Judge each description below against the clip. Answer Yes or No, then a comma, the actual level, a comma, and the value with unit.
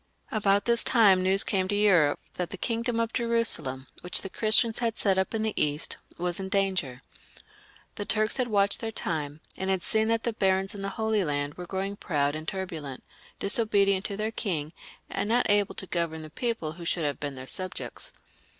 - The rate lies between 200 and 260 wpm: Yes, fast, 205 wpm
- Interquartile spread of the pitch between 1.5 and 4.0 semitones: No, average, 4.7 semitones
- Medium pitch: No, high, 195 Hz